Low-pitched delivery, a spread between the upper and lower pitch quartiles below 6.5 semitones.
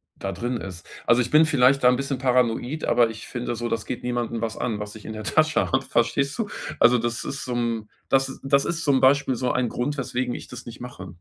Yes: low, 125 Hz; narrow, 2.5 semitones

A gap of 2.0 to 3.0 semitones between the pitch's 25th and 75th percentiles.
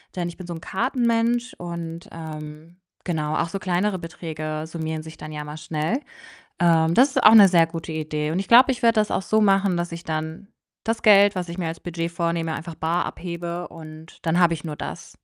No: average, 3.4 semitones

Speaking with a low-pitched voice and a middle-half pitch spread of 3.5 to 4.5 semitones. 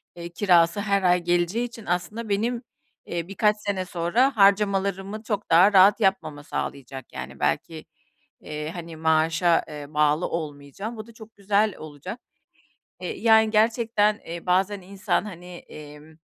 No: high, 190 Hz; average, 4.1 semitones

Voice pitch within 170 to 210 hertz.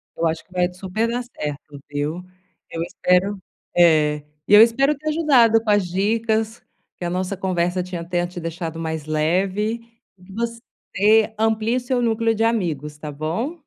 Yes: high, 190 Hz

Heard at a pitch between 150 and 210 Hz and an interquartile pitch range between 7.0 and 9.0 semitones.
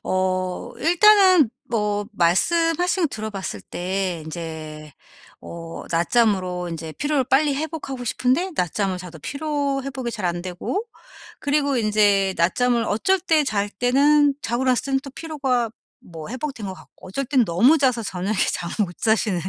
No: high, 230 Hz; wide, 7.5 semitones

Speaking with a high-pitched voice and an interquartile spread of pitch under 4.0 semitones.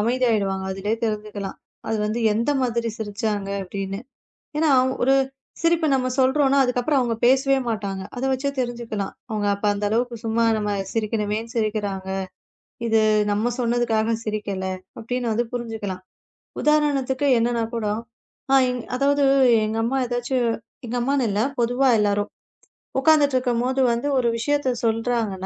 Yes: high, 230 Hz; average, 3.3 semitones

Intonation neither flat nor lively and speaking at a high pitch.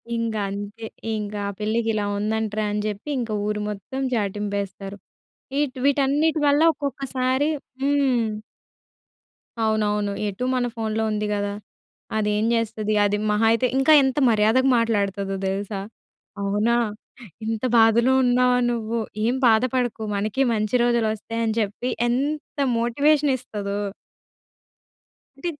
Yes: average, 3.4 semitones; high, 225 Hz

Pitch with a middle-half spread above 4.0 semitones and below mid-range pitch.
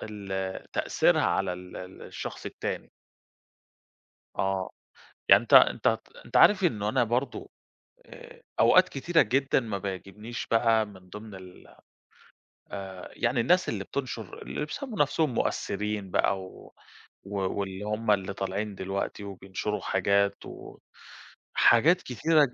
Yes: average, 4.7 semitones; low, 105 Hz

